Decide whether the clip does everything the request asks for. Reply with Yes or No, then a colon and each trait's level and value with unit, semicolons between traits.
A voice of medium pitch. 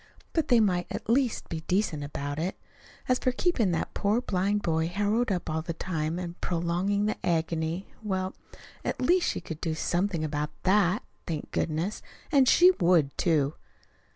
Yes: medium, 180 Hz